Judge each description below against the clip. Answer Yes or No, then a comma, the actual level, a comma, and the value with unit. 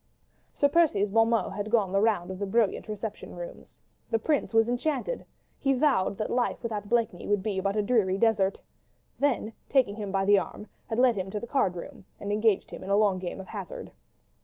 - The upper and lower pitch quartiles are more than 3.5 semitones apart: No, average, 3.2 semitones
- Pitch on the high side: Yes, high, 215 Hz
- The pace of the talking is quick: Yes, fast, 210 wpm